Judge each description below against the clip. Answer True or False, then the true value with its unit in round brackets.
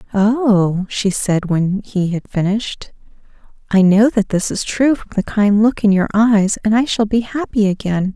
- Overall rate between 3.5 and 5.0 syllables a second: True (4.3 syllables/s)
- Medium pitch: False (205 Hz)